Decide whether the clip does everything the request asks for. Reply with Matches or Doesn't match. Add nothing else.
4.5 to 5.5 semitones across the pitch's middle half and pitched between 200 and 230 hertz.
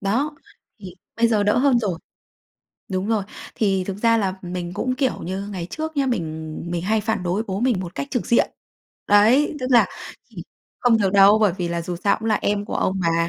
Doesn't match